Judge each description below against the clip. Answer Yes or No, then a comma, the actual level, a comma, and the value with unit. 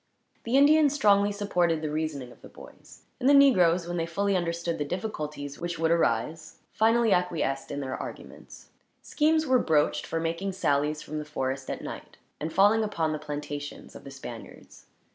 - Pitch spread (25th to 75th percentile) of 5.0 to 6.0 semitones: Yes, average, 5.3 semitones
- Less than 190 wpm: Yes, average, 180 wpm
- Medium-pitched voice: Yes, medium, 165 Hz